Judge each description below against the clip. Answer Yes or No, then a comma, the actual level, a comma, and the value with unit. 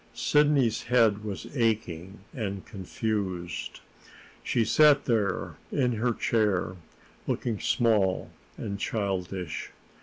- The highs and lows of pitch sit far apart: No, average, 3.6 semitones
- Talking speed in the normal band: No, slow, 95 wpm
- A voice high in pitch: No, low, 105 Hz